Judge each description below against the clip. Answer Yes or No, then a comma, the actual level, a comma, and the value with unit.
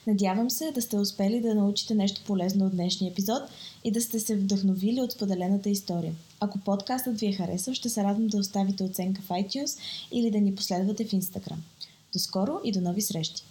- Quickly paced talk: Yes, fast, 200 wpm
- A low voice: No, high, 200 Hz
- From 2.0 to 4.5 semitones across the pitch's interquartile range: Yes, average, 2.9 semitones